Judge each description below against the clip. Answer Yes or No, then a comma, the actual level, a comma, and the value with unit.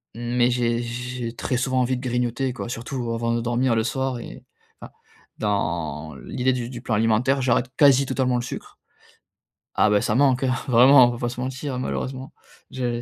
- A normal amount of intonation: No, narrow, 1.7 semitones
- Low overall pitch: Yes, low, 125 Hz